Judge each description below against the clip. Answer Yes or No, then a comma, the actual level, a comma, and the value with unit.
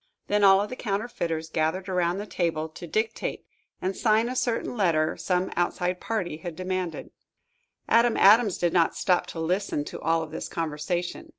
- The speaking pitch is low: No, medium, 180 Hz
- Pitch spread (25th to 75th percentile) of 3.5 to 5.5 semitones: Yes, average, 3.9 semitones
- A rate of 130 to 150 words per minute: No, average, 175 wpm